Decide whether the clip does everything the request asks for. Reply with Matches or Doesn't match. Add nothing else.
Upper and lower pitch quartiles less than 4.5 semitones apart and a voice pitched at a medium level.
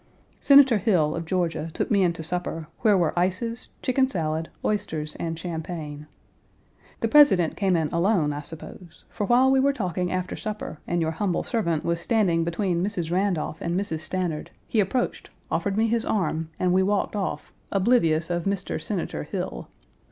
Matches